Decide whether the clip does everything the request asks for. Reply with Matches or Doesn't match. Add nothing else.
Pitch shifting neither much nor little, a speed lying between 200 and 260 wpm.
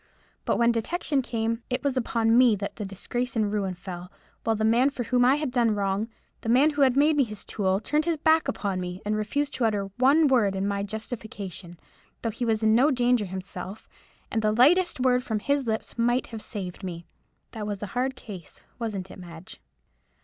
Matches